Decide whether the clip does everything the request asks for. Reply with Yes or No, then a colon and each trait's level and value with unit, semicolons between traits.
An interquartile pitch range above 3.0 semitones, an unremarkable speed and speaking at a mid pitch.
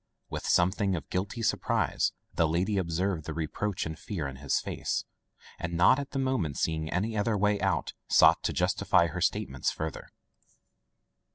No: average, 4.5 semitones; average, 165 wpm; very low, 90 Hz